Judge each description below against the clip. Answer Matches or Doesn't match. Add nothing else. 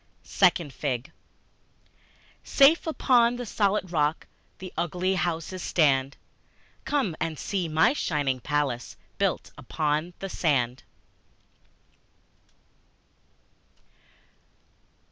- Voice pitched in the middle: Matches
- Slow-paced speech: Matches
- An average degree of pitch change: Matches